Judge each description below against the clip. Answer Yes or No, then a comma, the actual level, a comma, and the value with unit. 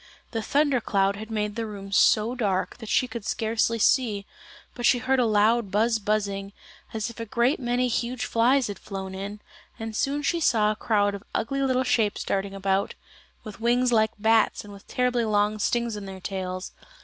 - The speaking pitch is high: Yes, high, 220 Hz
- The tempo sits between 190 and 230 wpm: Yes, average, 195 wpm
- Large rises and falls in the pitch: No, average, 2.9 semitones